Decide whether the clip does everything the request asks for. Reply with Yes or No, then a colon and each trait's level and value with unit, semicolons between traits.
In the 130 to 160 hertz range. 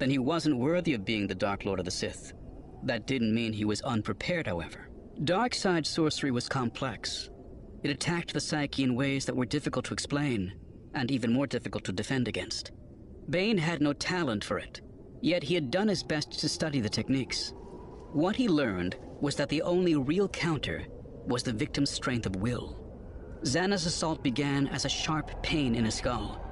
Yes: low, 135 Hz